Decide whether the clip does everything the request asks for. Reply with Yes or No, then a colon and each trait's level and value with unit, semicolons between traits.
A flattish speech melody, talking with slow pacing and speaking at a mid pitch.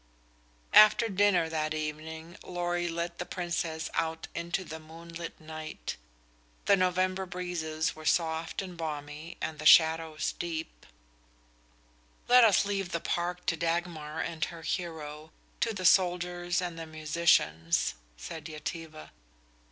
Yes: narrow, 2.0 semitones; slow, 130 wpm; medium, 165 Hz